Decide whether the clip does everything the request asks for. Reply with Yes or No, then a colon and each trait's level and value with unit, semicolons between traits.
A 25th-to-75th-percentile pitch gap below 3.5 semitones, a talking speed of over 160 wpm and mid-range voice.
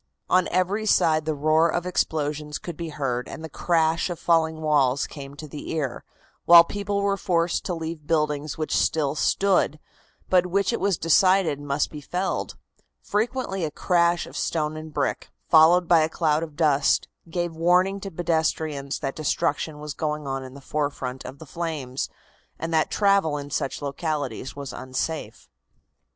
Yes: average, 3.0 semitones; average, 170 wpm; medium, 160 Hz